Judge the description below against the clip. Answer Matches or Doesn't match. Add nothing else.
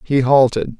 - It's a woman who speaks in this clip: Doesn't match